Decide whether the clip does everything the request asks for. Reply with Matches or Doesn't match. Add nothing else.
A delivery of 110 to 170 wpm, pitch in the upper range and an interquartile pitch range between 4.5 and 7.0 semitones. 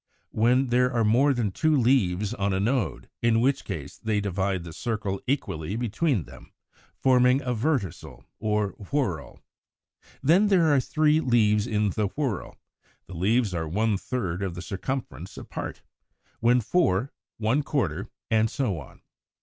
Doesn't match